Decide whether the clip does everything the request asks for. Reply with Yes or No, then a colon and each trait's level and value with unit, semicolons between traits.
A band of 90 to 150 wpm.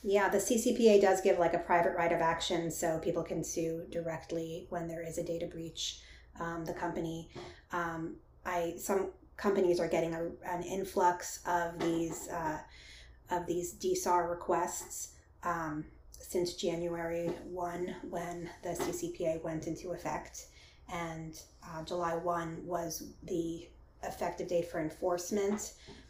Yes: average, 140 wpm